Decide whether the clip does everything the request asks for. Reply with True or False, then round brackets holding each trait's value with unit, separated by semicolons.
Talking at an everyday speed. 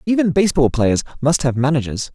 True (170 wpm)